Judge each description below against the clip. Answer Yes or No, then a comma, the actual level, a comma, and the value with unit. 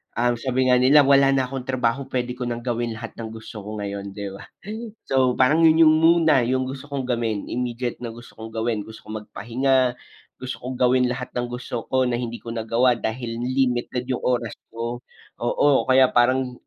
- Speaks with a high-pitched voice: No, low, 125 Hz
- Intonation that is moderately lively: No, narrow, 1.9 semitones